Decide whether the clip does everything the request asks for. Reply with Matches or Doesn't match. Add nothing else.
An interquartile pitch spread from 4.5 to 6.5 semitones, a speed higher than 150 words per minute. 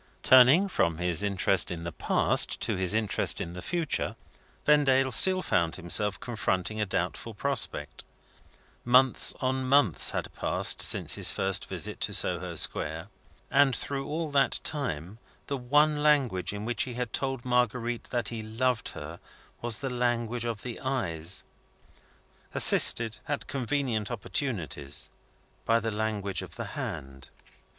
Doesn't match